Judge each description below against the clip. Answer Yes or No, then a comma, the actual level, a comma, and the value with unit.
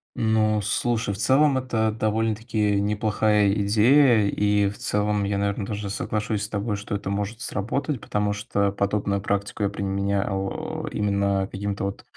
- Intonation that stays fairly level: Yes, narrow, 1.5 semitones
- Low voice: Yes, low, 105 Hz